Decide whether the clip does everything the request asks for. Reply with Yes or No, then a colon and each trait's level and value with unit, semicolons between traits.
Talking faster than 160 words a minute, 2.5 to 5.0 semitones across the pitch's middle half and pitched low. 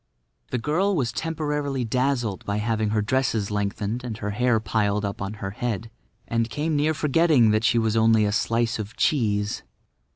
Yes: average, 175 wpm; average, 3.9 semitones; low, 115 Hz